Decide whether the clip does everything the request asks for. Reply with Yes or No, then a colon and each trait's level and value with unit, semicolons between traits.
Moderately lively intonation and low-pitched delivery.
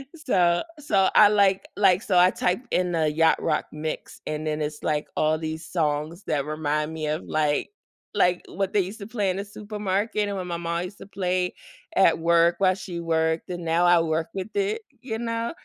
No: average, 3.8 semitones; medium, 175 Hz